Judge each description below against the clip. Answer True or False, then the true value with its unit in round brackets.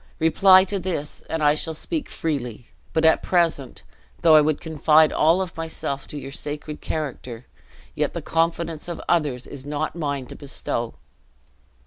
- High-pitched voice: False (155 Hz)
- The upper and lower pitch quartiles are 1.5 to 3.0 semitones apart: True (2.5 semitones)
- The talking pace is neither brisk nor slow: True (160 wpm)